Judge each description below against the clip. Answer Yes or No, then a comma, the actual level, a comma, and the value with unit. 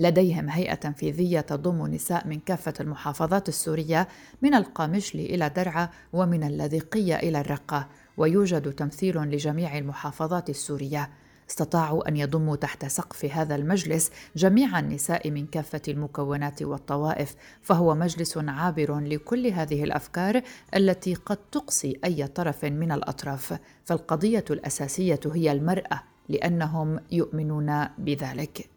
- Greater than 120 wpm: No, average, 115 wpm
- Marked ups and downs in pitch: No, average, 3.2 semitones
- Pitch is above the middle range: No, medium, 160 Hz